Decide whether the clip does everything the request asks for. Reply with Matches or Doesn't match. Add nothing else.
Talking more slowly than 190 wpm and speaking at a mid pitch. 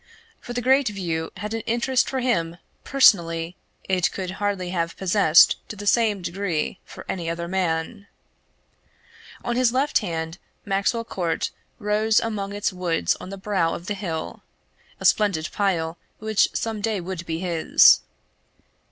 Doesn't match